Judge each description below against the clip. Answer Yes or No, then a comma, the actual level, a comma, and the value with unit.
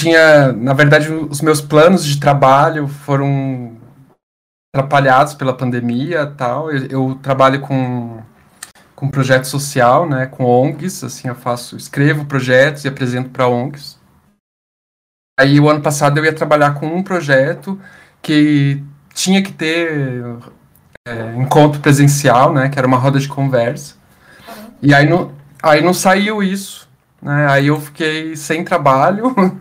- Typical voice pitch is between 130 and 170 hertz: Yes, medium, 140 Hz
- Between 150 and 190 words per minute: No, average, 140 wpm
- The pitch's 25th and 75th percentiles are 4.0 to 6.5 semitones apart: No, average, 3.1 semitones